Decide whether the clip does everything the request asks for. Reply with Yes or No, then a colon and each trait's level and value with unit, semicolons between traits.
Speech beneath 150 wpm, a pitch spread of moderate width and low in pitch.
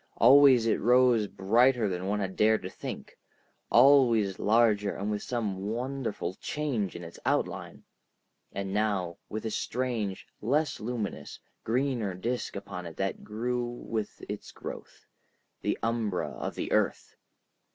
Yes: average, 140 wpm; average, 3.8 semitones; low, 110 Hz